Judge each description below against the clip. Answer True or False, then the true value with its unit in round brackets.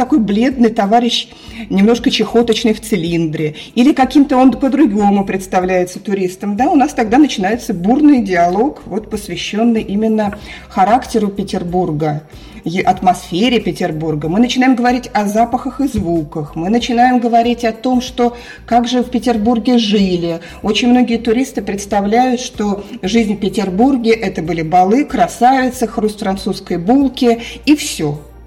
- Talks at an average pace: True (130 wpm)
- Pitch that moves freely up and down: False (4.3 semitones)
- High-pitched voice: True (225 Hz)